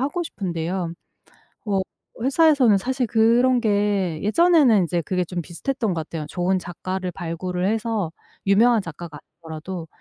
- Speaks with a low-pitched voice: No, high, 190 Hz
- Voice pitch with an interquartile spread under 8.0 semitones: Yes, average, 5.2 semitones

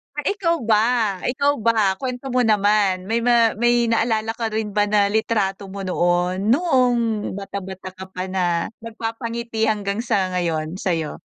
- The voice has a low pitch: No, high, 215 Hz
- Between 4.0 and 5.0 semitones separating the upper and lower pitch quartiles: No, average, 3.5 semitones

